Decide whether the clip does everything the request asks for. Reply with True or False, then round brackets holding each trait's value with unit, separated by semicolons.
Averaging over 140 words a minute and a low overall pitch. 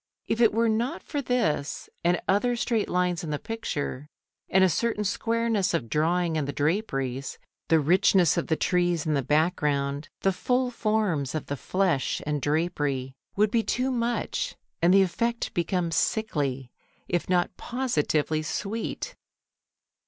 False (150 wpm; 180 Hz)